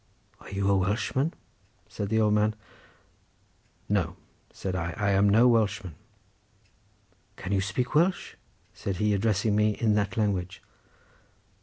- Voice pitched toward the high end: No, low, 105 Hz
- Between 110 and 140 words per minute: Yes, slow, 135 wpm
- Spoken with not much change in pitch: Yes, narrow, 2.0 semitones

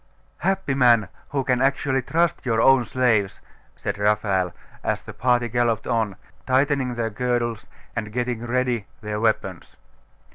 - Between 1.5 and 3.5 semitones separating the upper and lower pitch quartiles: Yes, average, 2.9 semitones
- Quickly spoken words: No, average, 140 wpm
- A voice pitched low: Yes, low, 120 Hz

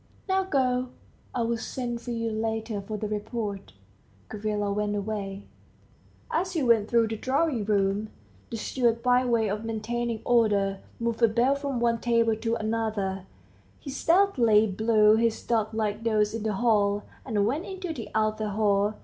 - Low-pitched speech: No, high, 225 Hz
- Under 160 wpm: No, average, 165 wpm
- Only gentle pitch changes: Yes, narrow, 2.2 semitones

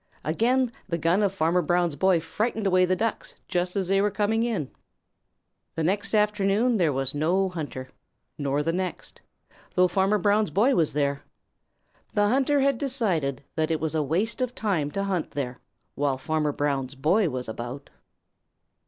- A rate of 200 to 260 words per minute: No, average, 170 wpm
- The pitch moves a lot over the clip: Yes, wide, 5.8 semitones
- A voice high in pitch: No, medium, 180 Hz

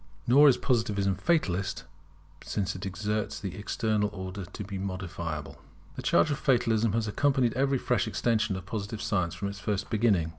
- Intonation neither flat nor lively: Yes, average, 3.6 semitones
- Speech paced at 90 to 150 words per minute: No, average, 165 wpm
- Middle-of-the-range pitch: No, low, 105 Hz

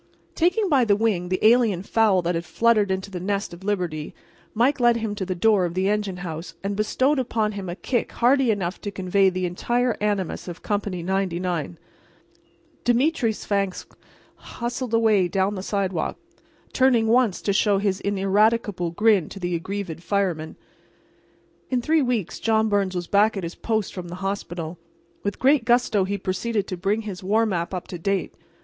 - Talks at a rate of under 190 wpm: Yes, average, 180 wpm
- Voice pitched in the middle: No, high, 200 Hz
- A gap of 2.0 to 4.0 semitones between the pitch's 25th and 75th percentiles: Yes, average, 3.5 semitones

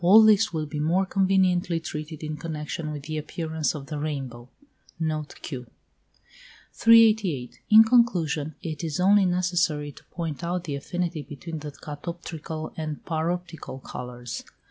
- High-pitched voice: No, medium, 160 Hz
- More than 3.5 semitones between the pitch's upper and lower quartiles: No, average, 3.1 semitones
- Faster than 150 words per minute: No, average, 145 wpm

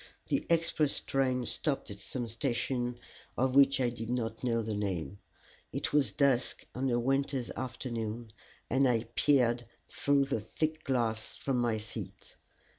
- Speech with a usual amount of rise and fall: Yes, average, 3.1 semitones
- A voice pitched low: Yes, low, 125 Hz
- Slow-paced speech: No, average, 150 wpm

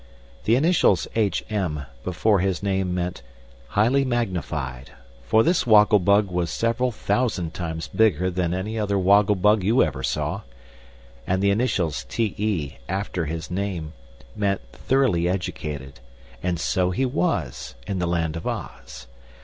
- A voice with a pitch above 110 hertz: No, very low, 95 Hz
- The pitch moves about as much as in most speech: Yes, average, 4.2 semitones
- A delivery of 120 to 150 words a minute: Yes, average, 145 wpm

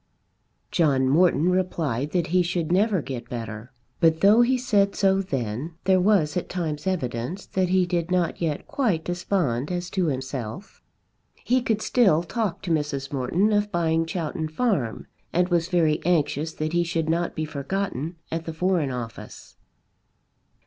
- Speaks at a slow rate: No, average, 160 wpm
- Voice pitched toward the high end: No, medium, 170 Hz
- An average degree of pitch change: Yes, average, 4.0 semitones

